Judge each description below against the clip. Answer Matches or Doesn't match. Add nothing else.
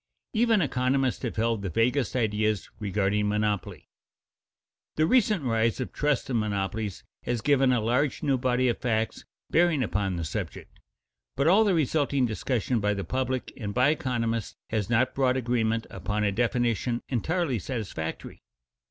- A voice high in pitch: Doesn't match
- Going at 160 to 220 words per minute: Doesn't match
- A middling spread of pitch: Matches